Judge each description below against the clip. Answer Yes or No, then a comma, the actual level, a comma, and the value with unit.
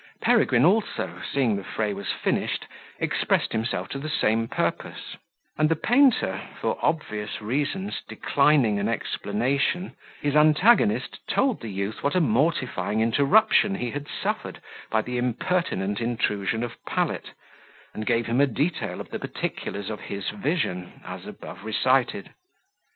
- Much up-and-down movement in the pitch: Yes, wide, 6.1 semitones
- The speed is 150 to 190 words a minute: No, average, 140 wpm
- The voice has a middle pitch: No, low, 125 Hz